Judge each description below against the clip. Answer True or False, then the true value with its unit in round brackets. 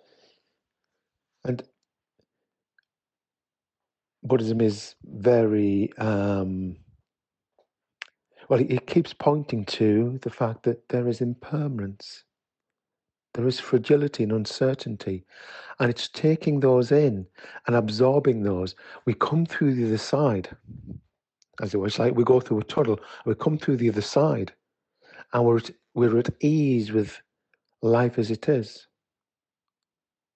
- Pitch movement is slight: False (3.8 semitones)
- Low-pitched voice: True (120 Hz)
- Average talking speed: False (120 wpm)